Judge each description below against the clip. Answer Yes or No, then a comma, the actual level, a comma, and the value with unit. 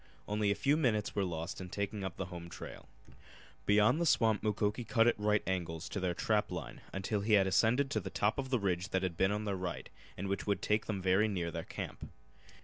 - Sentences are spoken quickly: Yes, fast, 235 wpm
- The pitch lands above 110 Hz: No, low, 100 Hz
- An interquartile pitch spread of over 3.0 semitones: No, narrow, 2.5 semitones